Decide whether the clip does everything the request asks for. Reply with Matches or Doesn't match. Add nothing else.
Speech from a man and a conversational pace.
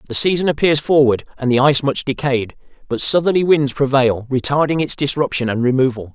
Matches